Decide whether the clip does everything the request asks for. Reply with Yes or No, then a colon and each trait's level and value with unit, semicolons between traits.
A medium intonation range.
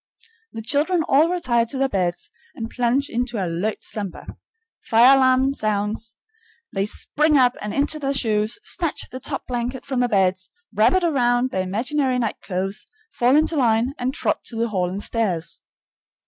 Yes: average, 4.3 semitones